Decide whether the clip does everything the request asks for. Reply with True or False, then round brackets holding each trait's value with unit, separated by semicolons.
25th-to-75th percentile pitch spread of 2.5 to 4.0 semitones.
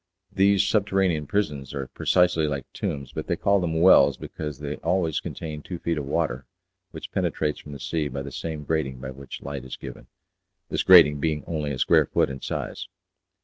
True (3.5 semitones)